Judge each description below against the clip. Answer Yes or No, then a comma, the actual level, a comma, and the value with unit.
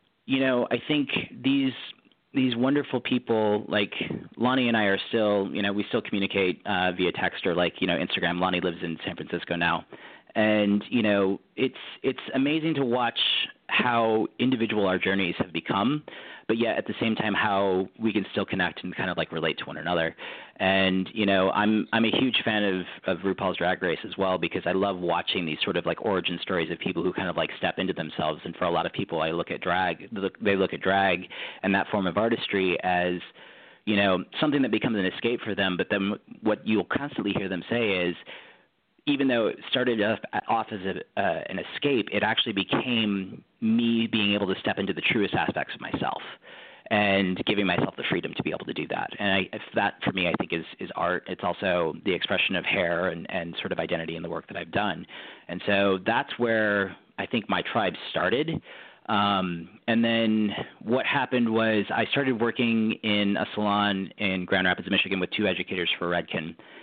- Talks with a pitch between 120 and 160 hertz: No, low, 100 Hz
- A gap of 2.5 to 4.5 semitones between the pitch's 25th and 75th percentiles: Yes, average, 3.3 semitones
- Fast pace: Yes, fast, 210 wpm